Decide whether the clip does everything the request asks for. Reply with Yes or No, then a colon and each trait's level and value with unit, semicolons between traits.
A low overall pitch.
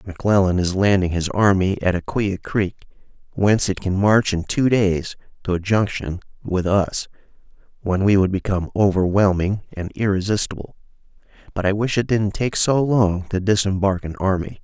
Yes: low, 100 Hz